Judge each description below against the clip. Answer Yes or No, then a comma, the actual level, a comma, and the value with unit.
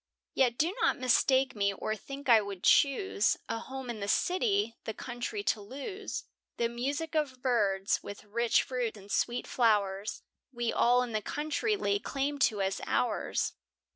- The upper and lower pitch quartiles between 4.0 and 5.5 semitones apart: Yes, average, 4.6 semitones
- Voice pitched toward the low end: No, high, 240 Hz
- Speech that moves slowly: No, average, 170 wpm